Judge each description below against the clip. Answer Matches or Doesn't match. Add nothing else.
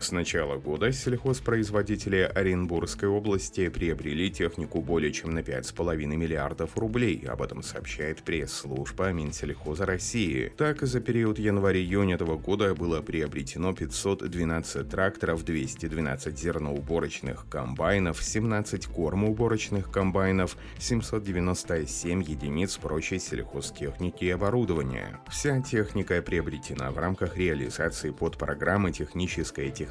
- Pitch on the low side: Matches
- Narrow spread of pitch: Doesn't match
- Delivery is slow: Matches